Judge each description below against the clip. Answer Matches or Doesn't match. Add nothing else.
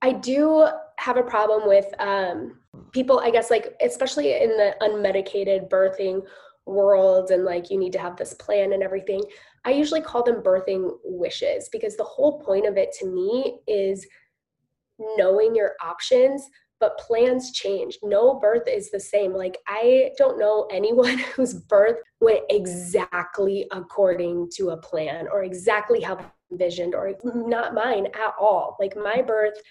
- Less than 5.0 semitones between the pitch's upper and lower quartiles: Doesn't match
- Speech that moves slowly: Doesn't match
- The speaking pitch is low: Doesn't match